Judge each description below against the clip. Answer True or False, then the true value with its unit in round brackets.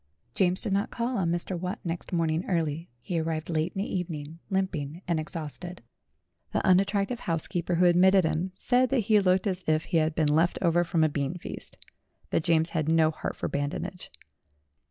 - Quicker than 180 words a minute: True (190 wpm)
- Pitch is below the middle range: False (170 Hz)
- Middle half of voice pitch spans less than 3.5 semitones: True (2.9 semitones)